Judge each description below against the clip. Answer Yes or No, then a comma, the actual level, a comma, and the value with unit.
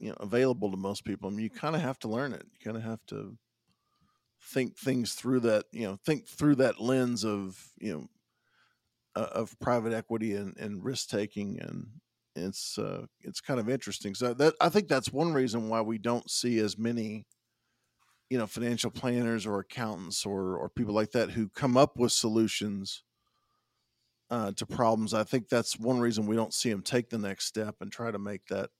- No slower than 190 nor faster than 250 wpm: Yes, fast, 205 wpm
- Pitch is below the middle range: Yes, low, 115 Hz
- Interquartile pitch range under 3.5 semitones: Yes, average, 2.9 semitones